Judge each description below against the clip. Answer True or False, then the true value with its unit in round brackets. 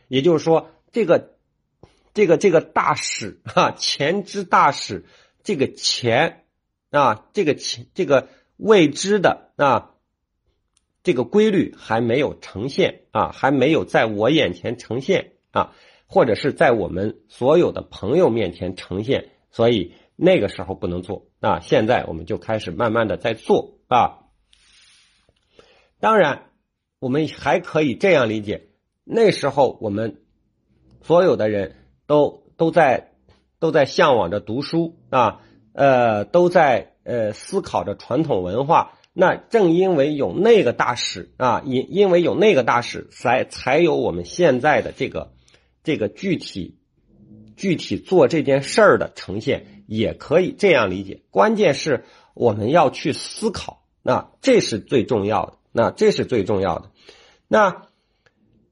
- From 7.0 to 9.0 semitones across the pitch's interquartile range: True (8.1 semitones)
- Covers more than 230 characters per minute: False (210 characters per minute)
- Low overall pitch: True (125 Hz)